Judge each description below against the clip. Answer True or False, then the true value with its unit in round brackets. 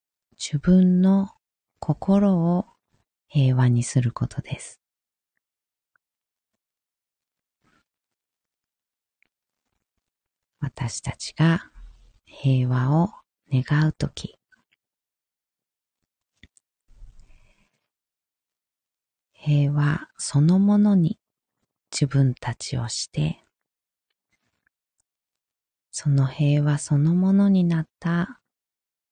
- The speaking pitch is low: False (145 Hz)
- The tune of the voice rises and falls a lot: True (6.0 semitones)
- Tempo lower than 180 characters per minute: True (105 characters per minute)